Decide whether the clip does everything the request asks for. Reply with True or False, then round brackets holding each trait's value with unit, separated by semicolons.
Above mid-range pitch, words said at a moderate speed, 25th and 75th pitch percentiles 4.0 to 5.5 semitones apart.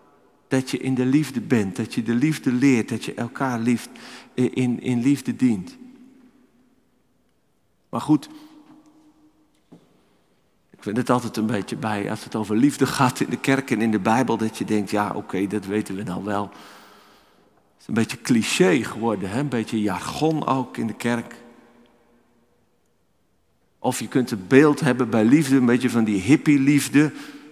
False (120 Hz; 170 wpm; 5.0 semitones)